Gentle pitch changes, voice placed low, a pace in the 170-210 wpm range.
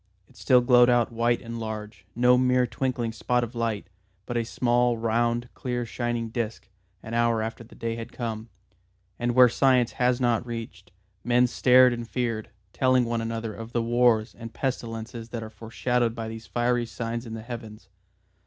Yes: narrow, 1.4 semitones; low, 120 Hz; average, 180 wpm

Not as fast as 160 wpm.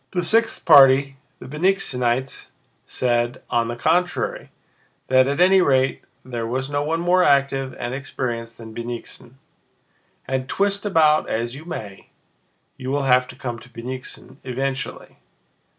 Yes: average, 140 wpm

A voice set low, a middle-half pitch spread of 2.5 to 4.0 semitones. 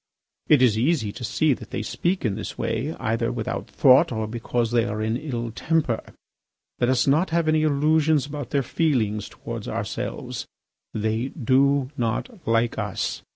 No: low, 125 Hz; average, 4.9 semitones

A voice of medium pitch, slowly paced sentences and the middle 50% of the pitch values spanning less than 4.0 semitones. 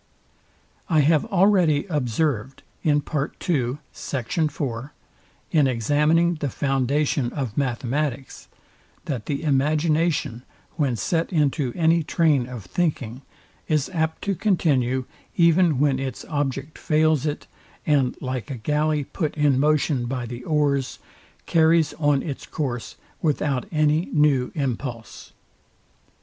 Yes: medium, 145 Hz; slow, 110 wpm; average, 3.2 semitones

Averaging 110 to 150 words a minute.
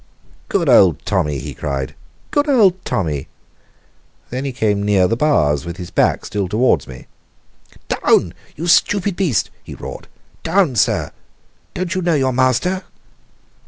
Yes: average, 145 wpm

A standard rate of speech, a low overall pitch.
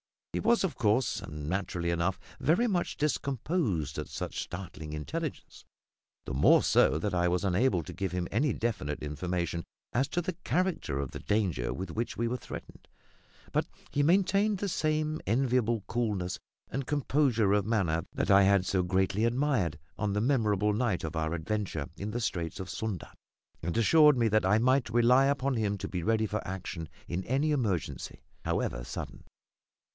Yes: average, 175 wpm; low, 105 Hz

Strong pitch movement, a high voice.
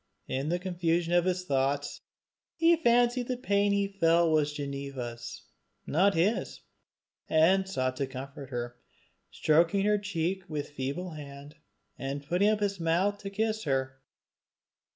No: wide, 6.1 semitones; medium, 165 Hz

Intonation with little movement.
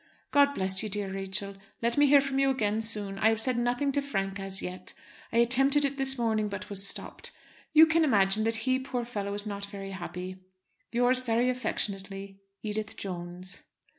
No: average, 4.7 semitones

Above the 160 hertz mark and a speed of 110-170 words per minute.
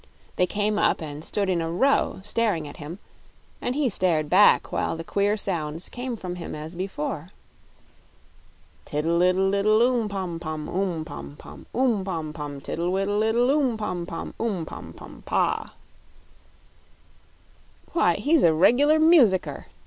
Yes: high, 190 Hz; average, 155 wpm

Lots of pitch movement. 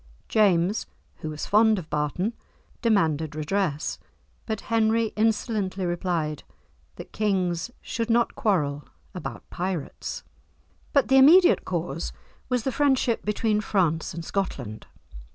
Yes: wide, 5.7 semitones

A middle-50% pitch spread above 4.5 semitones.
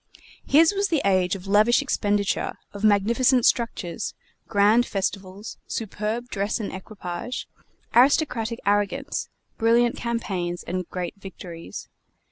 No: average, 3.7 semitones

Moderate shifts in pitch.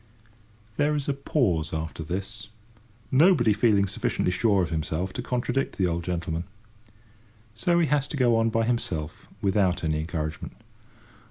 No: wide, 6.7 semitones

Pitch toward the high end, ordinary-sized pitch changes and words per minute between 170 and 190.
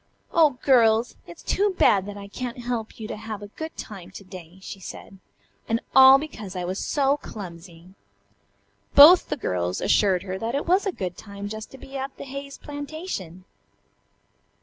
No: high, 220 Hz; wide, 6.6 semitones; average, 180 wpm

